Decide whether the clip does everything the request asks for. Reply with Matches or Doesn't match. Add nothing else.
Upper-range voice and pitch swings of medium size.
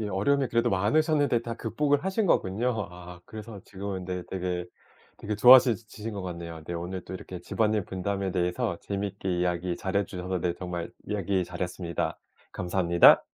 Doesn't match